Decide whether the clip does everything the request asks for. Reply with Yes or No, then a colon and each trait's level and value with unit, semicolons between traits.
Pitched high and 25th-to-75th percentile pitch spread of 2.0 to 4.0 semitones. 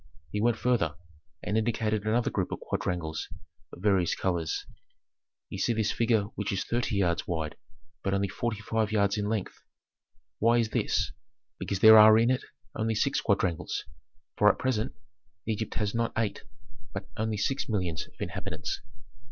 No: low, 105 Hz; narrow, 2.5 semitones